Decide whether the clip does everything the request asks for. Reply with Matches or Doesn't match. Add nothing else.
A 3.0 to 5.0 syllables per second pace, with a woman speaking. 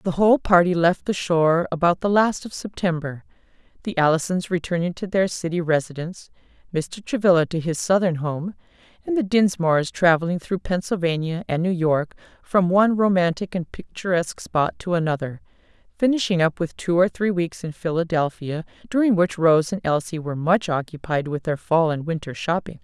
Doesn't match